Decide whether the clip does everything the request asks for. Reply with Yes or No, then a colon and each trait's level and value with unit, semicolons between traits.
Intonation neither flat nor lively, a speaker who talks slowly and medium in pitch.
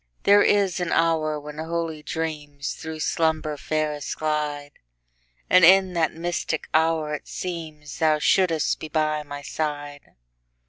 No: narrow, 1.8 semitones; slow, 120 wpm; medium, 155 Hz